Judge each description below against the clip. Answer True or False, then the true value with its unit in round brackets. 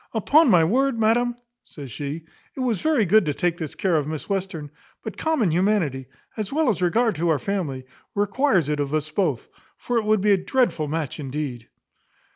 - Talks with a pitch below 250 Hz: True (185 Hz)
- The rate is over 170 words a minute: True (195 wpm)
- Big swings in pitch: True (6.8 semitones)